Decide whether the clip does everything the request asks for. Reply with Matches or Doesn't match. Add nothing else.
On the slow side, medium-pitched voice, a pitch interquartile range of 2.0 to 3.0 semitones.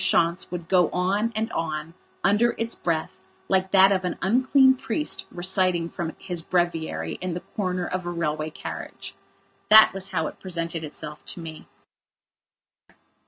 Doesn't match